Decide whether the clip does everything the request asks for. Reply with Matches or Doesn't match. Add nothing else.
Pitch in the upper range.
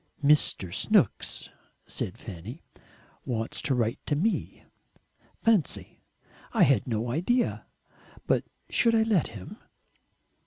Doesn't match